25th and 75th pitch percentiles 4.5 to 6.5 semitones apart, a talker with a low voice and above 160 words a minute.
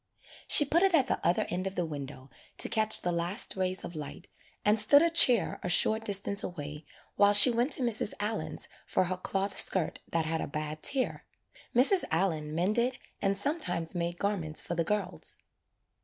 No: average, 4.9 semitones; high, 195 Hz; average, 185 wpm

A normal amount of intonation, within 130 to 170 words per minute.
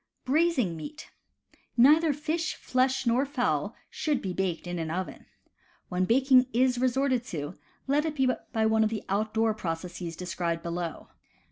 No: wide, 7.0 semitones; average, 155 wpm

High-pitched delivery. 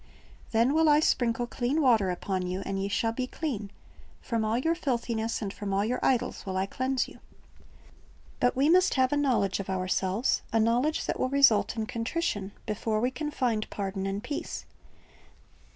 Yes: high, 230 Hz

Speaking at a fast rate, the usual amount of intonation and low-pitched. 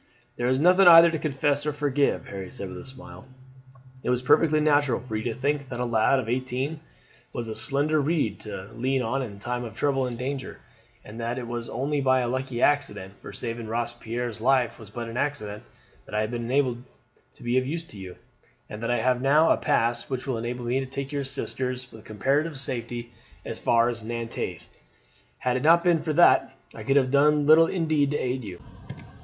Yes: fast, 215 wpm; average, 3.4 semitones; low, 130 Hz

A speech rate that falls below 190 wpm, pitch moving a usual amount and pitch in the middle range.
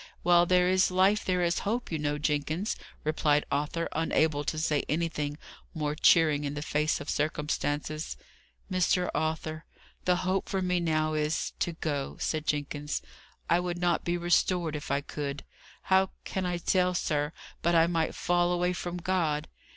Yes: average, 165 wpm; average, 3.0 semitones; medium, 165 Hz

